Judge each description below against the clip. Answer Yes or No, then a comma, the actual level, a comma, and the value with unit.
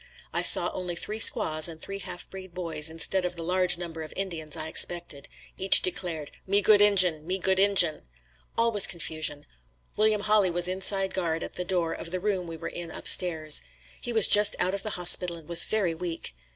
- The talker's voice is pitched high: No, medium, 180 Hz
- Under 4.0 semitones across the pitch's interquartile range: Yes, average, 2.7 semitones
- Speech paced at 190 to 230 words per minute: Yes, fast, 205 wpm